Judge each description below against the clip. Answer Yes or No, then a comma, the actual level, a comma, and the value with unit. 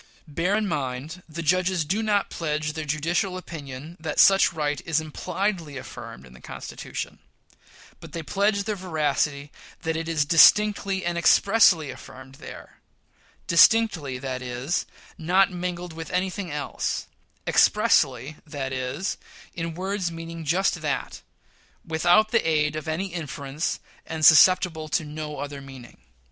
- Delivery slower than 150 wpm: Yes, average, 140 wpm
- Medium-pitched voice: Yes, medium, 160 Hz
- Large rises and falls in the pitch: No, average, 3.8 semitones